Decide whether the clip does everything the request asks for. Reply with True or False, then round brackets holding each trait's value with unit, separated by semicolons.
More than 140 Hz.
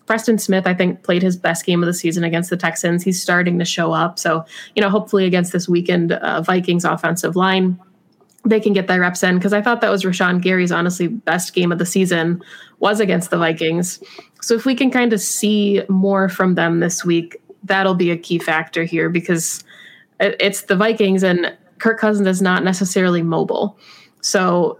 True (185 Hz)